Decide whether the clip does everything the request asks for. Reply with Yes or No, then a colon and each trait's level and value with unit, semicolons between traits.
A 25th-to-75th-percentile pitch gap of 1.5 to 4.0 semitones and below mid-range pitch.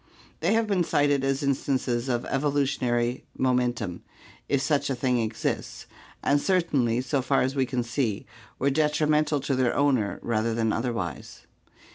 Yes: average, 3.2 semitones; low, 130 Hz